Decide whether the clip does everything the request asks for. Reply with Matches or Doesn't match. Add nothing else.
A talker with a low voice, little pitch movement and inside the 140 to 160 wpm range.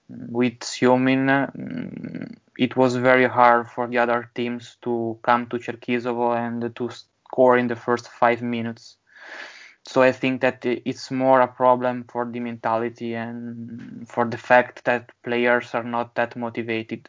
Matches